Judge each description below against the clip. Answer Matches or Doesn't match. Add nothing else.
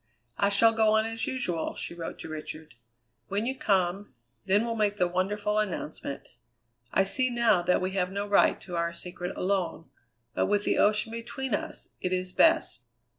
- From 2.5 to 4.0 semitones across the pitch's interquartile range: Matches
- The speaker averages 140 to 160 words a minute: Doesn't match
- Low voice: Doesn't match